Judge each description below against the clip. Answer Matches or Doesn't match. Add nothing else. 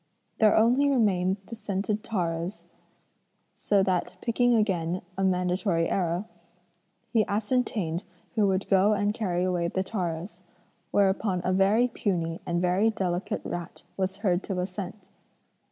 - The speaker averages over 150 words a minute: Doesn't match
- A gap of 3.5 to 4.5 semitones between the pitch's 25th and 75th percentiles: Doesn't match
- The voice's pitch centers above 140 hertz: Matches